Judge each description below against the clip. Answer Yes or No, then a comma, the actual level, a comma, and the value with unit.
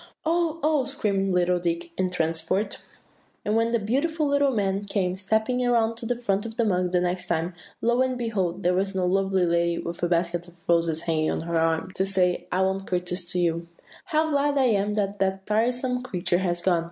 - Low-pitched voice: No, high, 190 Hz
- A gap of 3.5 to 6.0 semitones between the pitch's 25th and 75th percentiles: Yes, average, 4.8 semitones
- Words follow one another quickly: Yes, fast, 215 wpm